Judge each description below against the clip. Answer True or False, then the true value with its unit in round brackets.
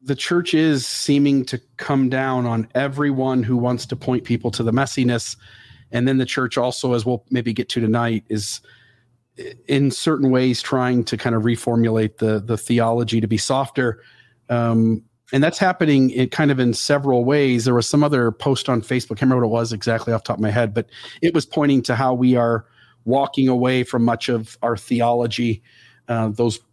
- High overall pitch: False (125 Hz)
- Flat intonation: True (2.2 semitones)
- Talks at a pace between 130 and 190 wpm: False (200 wpm)